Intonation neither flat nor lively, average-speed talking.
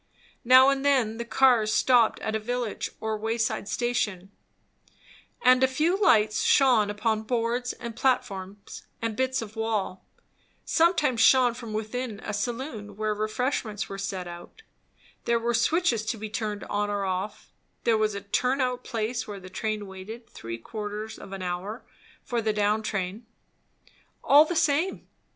Yes: average, 3.2 semitones; average, 160 wpm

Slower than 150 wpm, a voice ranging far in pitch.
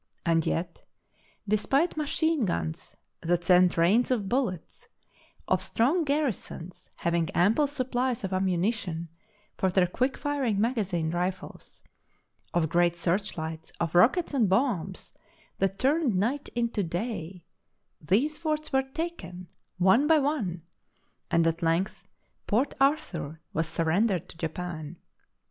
Yes: average, 140 wpm; wide, 7.3 semitones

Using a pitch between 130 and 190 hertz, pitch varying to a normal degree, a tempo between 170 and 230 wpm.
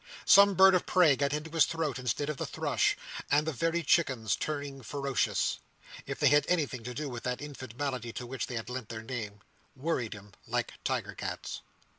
Yes: medium, 140 Hz; average, 3.8 semitones; average, 185 wpm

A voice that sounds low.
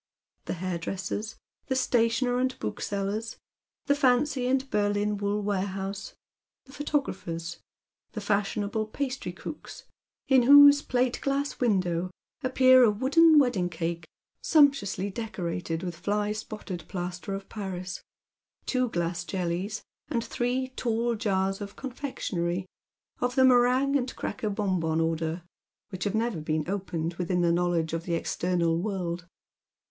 No: high, 205 Hz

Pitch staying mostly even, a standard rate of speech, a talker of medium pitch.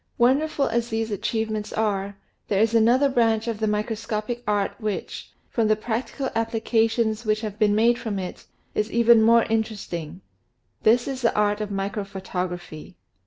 No: narrow, 2.0 semitones; average, 160 wpm; high, 220 Hz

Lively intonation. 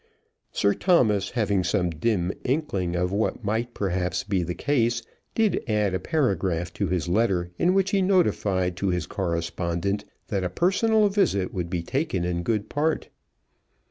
Yes: wide, 6.6 semitones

